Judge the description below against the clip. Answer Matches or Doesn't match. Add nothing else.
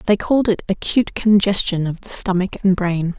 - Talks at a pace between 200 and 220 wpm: Doesn't match